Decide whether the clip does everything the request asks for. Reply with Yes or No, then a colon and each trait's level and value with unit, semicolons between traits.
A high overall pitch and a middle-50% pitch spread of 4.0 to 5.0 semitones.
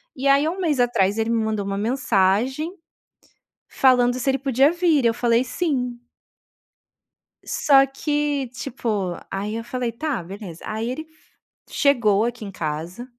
Yes: high, 245 Hz; average, 4.4 semitones